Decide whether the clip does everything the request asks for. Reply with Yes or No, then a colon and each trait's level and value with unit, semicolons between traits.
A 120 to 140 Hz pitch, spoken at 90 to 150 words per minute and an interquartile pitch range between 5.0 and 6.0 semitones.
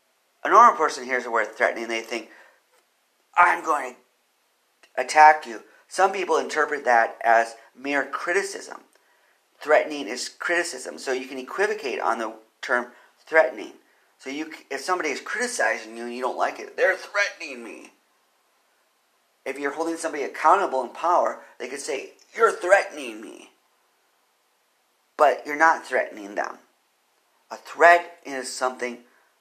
Yes: low, 135 Hz; average, 140 wpm; average, 5.3 semitones